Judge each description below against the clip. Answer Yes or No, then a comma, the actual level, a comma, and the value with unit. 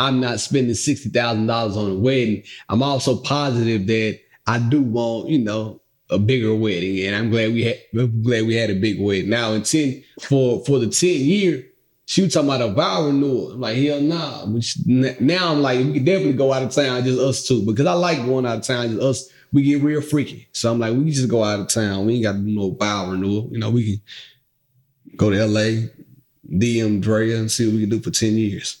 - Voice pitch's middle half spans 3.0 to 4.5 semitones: Yes, average, 3.8 semitones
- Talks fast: Yes, fast, 240 wpm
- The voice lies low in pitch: Yes, low, 120 Hz